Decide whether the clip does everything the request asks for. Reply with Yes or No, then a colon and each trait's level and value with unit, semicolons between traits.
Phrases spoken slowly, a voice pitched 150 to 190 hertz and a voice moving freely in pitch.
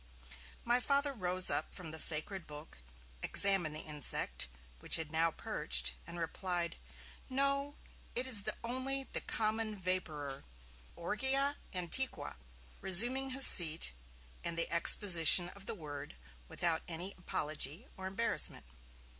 Yes: slow, 125 wpm; medium, 185 Hz; wide, 6.8 semitones